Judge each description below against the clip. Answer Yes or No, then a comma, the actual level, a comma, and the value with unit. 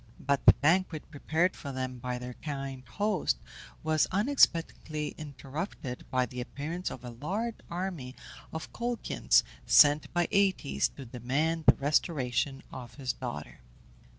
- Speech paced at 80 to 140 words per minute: Yes, slow, 135 wpm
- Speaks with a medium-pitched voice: Yes, medium, 145 Hz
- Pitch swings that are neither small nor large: Yes, average, 5.0 semitones